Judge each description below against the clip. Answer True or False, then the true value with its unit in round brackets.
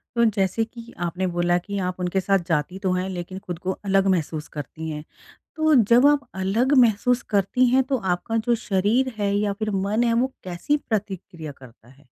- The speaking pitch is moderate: False (195 Hz)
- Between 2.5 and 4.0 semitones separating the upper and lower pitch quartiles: False (4.8 semitones)